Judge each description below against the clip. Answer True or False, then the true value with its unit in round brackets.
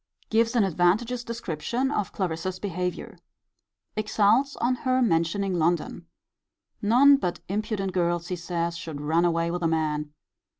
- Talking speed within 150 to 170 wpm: False (135 wpm)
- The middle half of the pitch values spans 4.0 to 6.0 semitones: True (5.1 semitones)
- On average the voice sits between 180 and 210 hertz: True (185 Hz)